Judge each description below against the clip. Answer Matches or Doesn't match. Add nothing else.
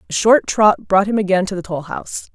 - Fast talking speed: Matches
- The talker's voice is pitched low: Doesn't match